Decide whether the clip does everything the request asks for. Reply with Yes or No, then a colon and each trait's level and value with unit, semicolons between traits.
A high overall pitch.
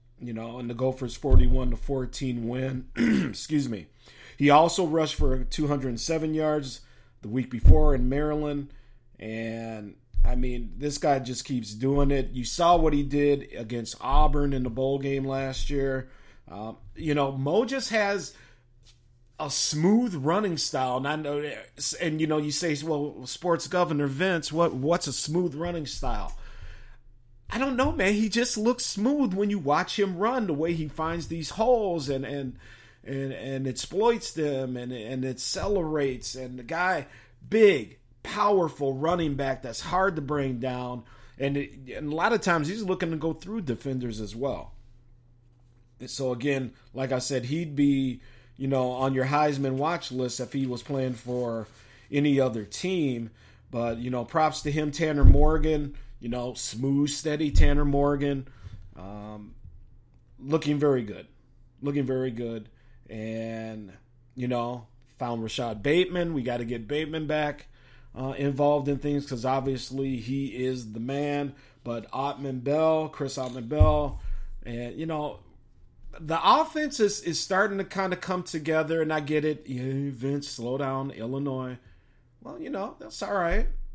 No: low, 135 Hz